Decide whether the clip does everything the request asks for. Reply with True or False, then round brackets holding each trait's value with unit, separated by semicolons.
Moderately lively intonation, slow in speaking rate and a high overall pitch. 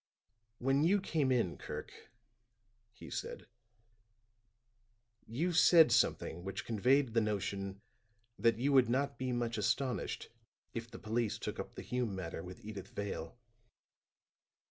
False (4.8 semitones; 130 wpm; 115 Hz)